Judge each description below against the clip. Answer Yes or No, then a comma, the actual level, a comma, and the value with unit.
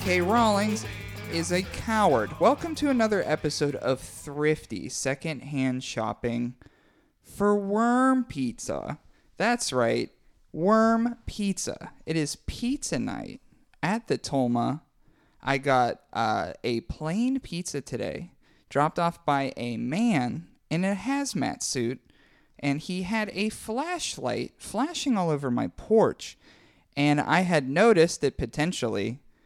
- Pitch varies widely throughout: Yes, wide, 8.8 semitones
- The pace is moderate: No, slow, 120 wpm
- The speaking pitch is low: No, medium, 160 Hz